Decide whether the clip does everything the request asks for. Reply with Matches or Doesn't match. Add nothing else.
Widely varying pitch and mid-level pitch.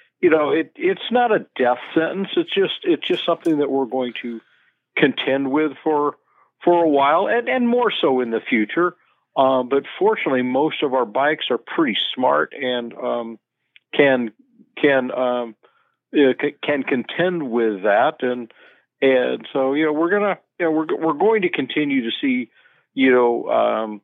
Matches